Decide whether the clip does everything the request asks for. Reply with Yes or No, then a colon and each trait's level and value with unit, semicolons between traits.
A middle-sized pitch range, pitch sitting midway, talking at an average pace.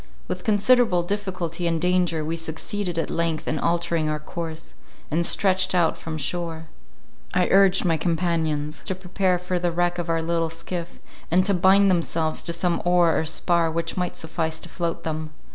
No: narrow, 1.8 semitones; medium, 170 Hz; average, 180 wpm